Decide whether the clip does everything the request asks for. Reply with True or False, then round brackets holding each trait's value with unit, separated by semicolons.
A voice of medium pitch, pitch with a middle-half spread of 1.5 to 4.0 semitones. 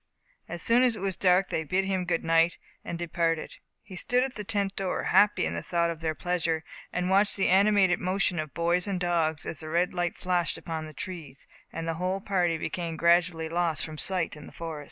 True (175 Hz; 2.4 semitones)